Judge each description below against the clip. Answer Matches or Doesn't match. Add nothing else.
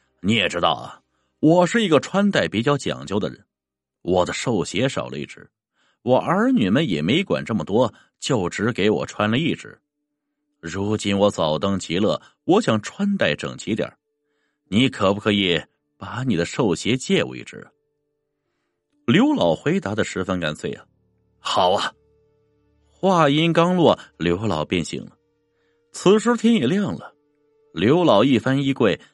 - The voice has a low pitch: Doesn't match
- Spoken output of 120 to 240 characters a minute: Matches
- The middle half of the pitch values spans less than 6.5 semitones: Doesn't match